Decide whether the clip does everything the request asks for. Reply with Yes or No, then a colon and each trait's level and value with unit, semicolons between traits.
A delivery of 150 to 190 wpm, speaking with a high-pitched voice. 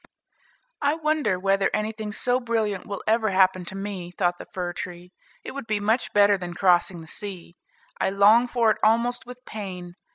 Yes: average, 185 wpm; high, 205 Hz